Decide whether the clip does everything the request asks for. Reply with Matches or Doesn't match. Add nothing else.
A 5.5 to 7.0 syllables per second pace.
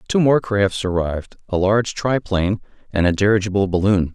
Matches